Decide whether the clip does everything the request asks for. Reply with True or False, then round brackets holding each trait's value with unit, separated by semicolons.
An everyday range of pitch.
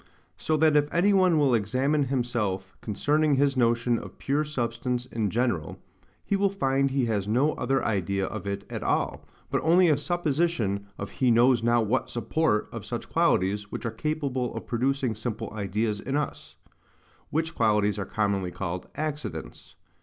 False (5.8 semitones)